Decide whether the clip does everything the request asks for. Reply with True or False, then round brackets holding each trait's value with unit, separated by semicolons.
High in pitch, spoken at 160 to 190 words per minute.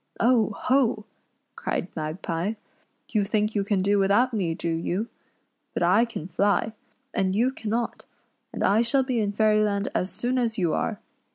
True (210 Hz; 180 wpm)